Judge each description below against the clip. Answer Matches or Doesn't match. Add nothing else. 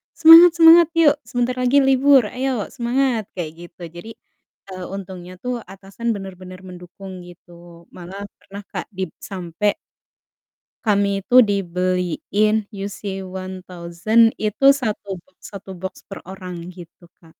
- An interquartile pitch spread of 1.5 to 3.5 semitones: Doesn't match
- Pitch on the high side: Matches